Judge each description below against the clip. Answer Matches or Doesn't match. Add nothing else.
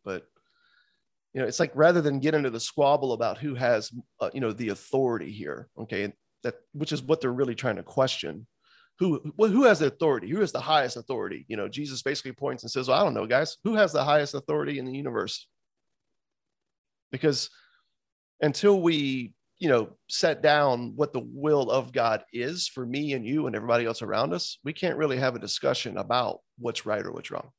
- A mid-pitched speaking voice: Matches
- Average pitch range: Matches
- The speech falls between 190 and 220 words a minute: Matches